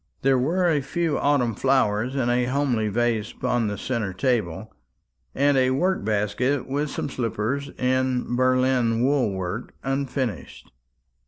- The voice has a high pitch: No, low, 130 Hz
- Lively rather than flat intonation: No, average, 3.0 semitones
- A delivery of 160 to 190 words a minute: No, average, 140 wpm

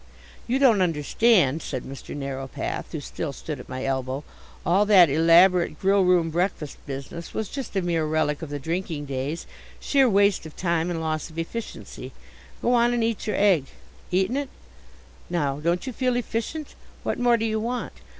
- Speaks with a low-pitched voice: No, medium, 175 Hz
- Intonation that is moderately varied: No, wide, 6.4 semitones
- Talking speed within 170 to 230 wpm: Yes, average, 180 wpm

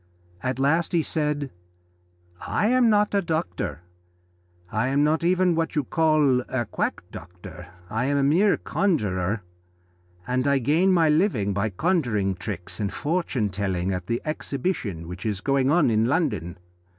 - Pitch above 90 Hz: Yes, low, 135 Hz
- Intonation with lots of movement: Yes, wide, 8.1 semitones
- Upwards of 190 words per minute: No, average, 155 wpm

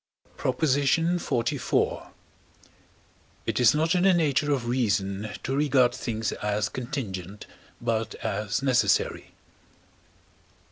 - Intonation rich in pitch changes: No, average, 4.9 semitones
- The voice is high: No, low, 125 Hz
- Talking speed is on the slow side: Yes, slow, 100 wpm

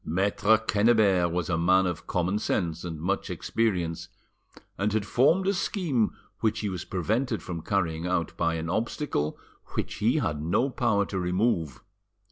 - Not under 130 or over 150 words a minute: No, average, 160 wpm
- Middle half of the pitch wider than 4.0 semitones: Yes, average, 4.5 semitones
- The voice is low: Yes, very low, 95 Hz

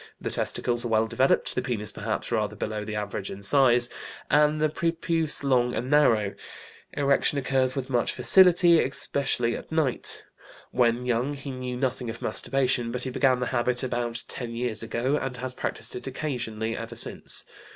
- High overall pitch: No, low, 125 Hz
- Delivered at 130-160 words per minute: No, average, 170 wpm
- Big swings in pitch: No, average, 2.8 semitones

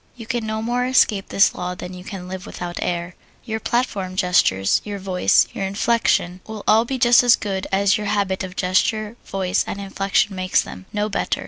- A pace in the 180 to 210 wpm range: Yes, average, 200 wpm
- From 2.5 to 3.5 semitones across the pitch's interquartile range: Yes, average, 2.9 semitones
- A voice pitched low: No, high, 200 Hz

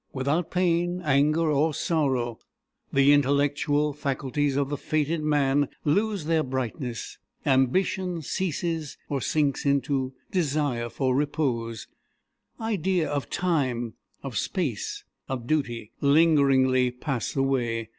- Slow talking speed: Yes, slow, 110 wpm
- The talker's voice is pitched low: No, medium, 145 Hz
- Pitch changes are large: No, average, 3.1 semitones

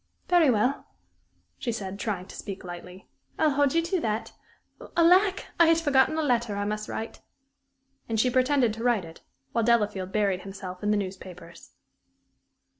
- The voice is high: Yes, high, 220 Hz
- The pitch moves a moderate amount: No, wide, 6.2 semitones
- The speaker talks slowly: No, average, 165 wpm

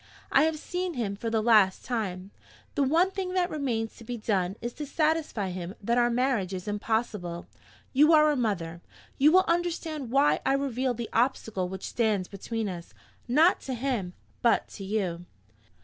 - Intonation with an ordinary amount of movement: No, wide, 6.5 semitones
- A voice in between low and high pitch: No, high, 235 Hz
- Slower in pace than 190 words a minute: Yes, average, 180 wpm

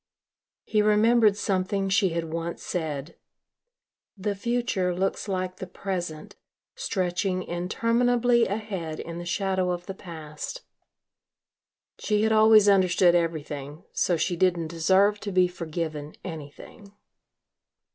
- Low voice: No, medium, 185 Hz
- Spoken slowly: Yes, slow, 115 wpm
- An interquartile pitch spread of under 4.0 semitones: Yes, average, 3.5 semitones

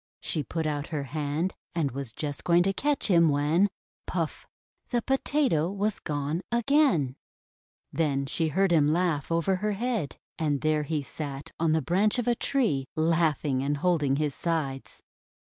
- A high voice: No, medium, 160 Hz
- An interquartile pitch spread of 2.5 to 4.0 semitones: No, average, 4.7 semitones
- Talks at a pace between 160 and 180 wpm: Yes, average, 165 wpm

